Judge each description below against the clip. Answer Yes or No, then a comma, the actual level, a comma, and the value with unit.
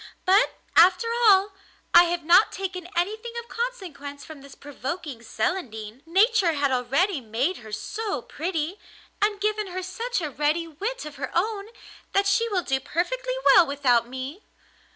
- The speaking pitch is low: No, very high, 345 Hz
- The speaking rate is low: No, average, 155 wpm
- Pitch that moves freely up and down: Yes, wide, 6.1 semitones